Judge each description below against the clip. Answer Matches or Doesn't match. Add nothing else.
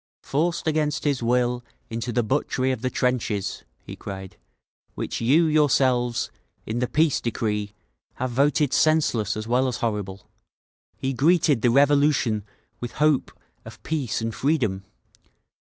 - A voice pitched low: Matches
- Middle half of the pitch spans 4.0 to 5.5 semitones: Matches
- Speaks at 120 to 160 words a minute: Matches